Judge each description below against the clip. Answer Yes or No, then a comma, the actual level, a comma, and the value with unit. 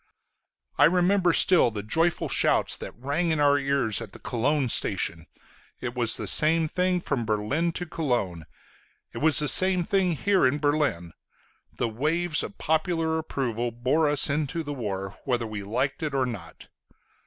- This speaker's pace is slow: No, average, 165 wpm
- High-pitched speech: No, medium, 145 Hz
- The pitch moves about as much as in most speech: No, wide, 5.7 semitones